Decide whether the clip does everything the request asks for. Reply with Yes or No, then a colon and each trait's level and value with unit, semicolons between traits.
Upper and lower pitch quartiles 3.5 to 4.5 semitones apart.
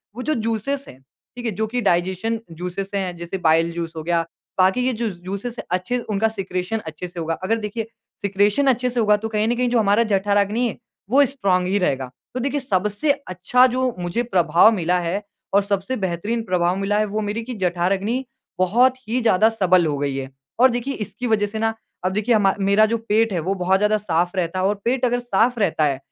Yes: average, 4.2 semitones